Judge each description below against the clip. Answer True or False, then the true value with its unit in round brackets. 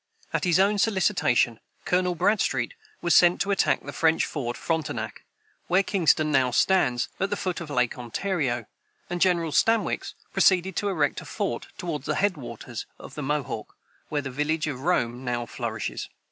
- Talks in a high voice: False (160 Hz)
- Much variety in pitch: True (6.4 semitones)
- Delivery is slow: False (170 wpm)